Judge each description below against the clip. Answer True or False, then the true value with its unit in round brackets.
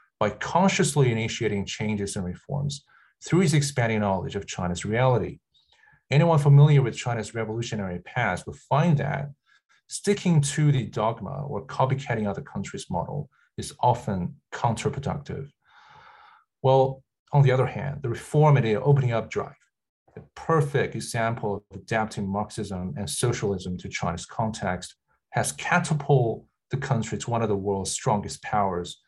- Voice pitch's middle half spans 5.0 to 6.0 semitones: True (5.4 semitones)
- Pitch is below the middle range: True (120 Hz)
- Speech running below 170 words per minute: True (140 wpm)